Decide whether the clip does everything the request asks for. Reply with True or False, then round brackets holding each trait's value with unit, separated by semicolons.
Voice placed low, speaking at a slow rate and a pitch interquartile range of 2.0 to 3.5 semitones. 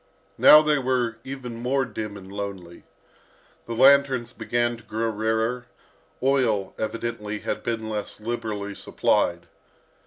True (115 Hz; 125 wpm; 2.9 semitones)